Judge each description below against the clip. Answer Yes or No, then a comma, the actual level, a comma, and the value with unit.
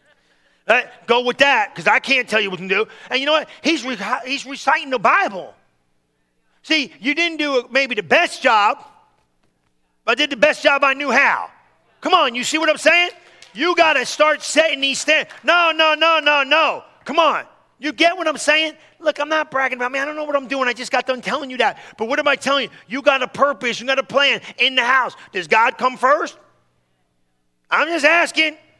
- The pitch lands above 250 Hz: Yes, very high, 280 Hz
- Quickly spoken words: Yes, fast, 225 wpm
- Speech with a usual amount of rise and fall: Yes, average, 3.5 semitones